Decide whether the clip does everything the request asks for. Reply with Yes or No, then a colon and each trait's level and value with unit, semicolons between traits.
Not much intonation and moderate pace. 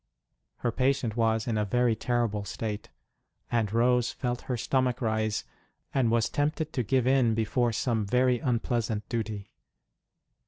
Yes: narrow, 2.2 semitones; average, 145 wpm